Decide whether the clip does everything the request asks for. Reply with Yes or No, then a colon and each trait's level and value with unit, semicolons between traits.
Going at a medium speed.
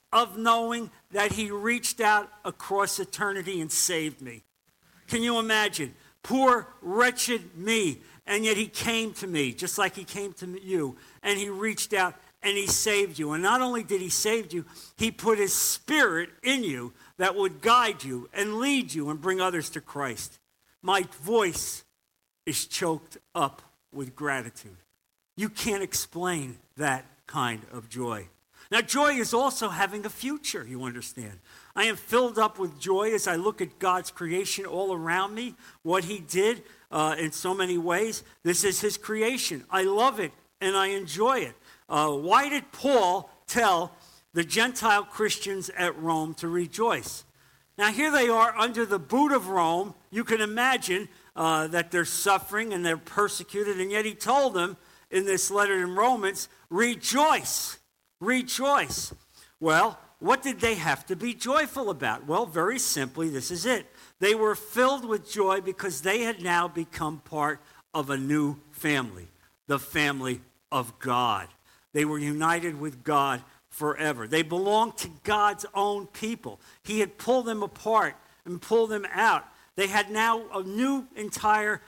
Yes: average, 165 wpm